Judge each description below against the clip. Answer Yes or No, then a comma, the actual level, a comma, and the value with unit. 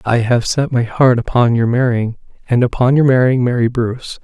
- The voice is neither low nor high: No, low, 120 Hz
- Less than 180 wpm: No, average, 200 wpm